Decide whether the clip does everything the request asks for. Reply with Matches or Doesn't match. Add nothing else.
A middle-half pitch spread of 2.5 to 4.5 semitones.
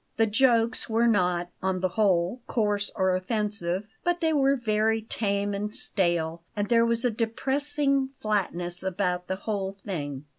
Matches